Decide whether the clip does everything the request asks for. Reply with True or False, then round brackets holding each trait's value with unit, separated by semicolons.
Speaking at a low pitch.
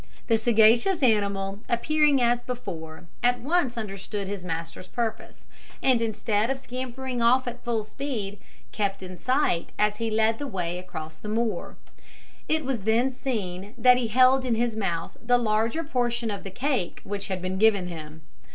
False (225 Hz)